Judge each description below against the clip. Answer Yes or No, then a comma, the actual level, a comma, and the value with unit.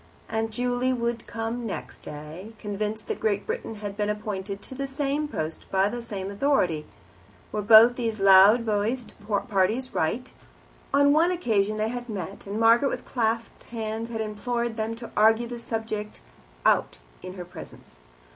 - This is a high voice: Yes, high, 220 Hz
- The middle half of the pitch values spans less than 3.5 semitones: Yes, average, 2.9 semitones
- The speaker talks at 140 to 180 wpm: Yes, average, 165 wpm